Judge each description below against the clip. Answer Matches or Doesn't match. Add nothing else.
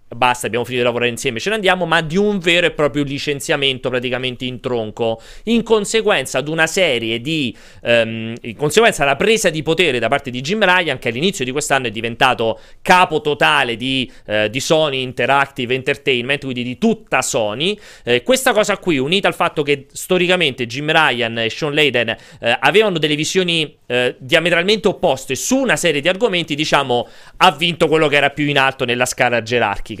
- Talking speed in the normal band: Doesn't match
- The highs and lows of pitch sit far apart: Matches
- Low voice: Doesn't match